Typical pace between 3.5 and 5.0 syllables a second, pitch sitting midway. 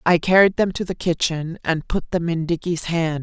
Yes: 4.9 syllables/s; medium, 170 Hz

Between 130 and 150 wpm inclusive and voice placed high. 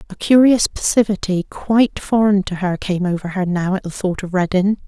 No: average, 195 wpm; high, 195 Hz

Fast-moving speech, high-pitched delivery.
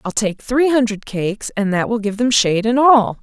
Yes: fast, 240 wpm; high, 225 Hz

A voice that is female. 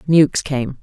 Yes: female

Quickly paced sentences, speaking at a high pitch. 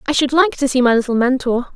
Yes: fast, 275 wpm; very high, 270 Hz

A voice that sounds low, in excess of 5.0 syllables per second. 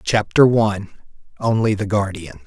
No: low, 105 Hz; 4.9 syllables/s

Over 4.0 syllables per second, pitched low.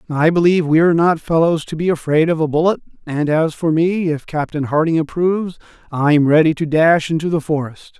No: 5.4 syllables/s; medium, 160 Hz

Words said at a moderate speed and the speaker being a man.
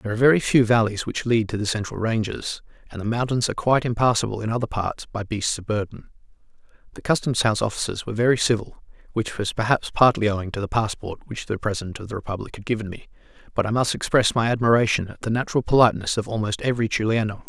No: fast, 215 wpm; male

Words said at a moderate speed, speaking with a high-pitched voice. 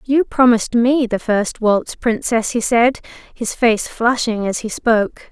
Yes: average, 170 wpm; high, 230 Hz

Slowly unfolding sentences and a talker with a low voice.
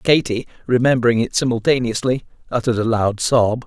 Yes: slow, 130 wpm; low, 120 Hz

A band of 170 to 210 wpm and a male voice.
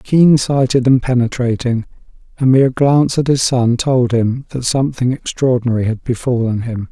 No: average, 155 wpm; male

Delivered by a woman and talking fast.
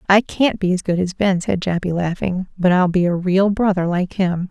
Yes: female; fast, 240 wpm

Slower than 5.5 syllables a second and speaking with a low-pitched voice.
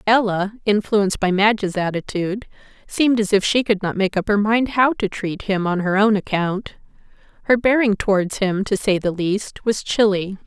No: 5.0 syllables/s; high, 205 Hz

